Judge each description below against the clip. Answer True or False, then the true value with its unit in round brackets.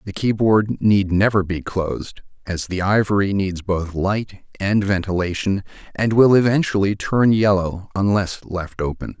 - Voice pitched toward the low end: True (100 Hz)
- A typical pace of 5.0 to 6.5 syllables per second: False (4.3 syllables/s)